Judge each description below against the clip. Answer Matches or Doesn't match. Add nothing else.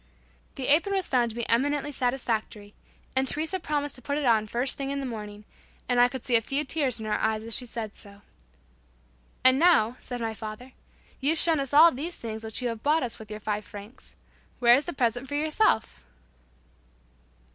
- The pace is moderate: Doesn't match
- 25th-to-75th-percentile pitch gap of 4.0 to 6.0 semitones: Matches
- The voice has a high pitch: Matches